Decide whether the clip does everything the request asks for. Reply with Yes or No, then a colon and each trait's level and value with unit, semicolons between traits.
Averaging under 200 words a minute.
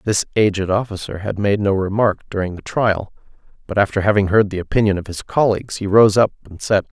No: fast, 205 wpm